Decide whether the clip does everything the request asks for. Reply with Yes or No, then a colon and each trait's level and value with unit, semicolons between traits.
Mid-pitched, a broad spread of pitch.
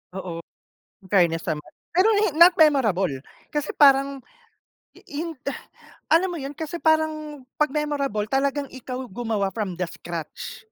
No: very high, 275 Hz; wide, 7.3 semitones